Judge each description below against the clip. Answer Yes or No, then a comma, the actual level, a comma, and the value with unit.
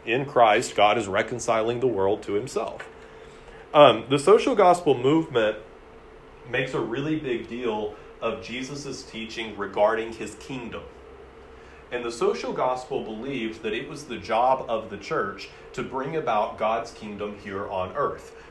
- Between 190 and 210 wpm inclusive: No, average, 150 wpm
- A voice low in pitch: No, medium, 145 Hz